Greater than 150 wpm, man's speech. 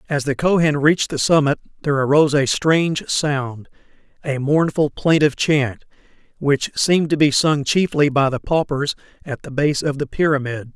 Yes: average, 160 wpm; male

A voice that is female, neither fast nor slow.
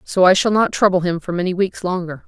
No: female; fast, 265 wpm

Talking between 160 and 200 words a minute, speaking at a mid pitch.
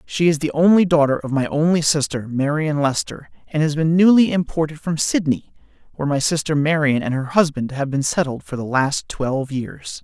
Yes: average, 195 wpm; medium, 150 Hz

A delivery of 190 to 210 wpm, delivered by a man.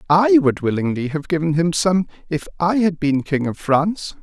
Yes: average, 200 wpm; male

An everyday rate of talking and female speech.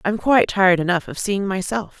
No: fast, 240 wpm; female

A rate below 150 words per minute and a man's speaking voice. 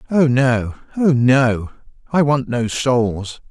Yes: slow, 135 wpm; male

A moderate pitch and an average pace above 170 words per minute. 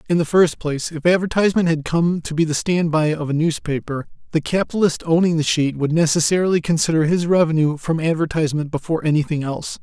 Yes: medium, 160 Hz; average, 190 wpm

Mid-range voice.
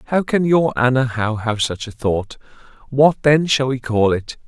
No: low, 125 Hz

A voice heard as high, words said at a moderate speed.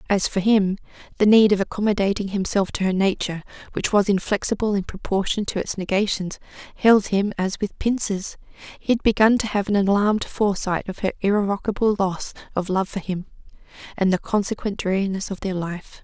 Yes: high, 200 Hz; average, 175 wpm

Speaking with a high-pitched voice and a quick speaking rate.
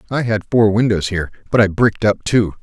No: low, 105 Hz; fast, 230 wpm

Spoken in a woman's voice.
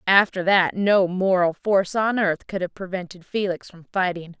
Yes: female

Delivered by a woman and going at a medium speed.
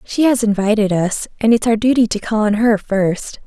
No: female; fast, 225 wpm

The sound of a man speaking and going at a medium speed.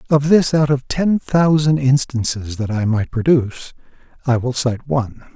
Yes: male; average, 170 wpm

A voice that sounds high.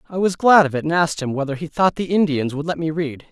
No: medium, 160 Hz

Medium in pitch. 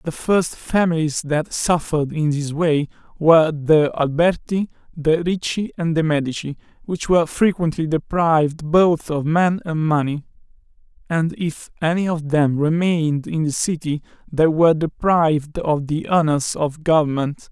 Yes: medium, 160 Hz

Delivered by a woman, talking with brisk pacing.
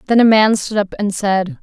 Yes: female; fast, 260 wpm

